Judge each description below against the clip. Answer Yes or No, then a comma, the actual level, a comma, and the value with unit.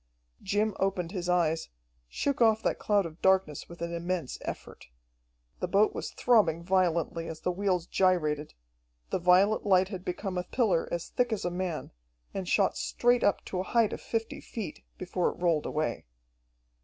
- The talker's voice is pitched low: No, medium, 185 Hz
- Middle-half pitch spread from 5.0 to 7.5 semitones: No, average, 3.0 semitones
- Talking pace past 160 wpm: Yes, average, 175 wpm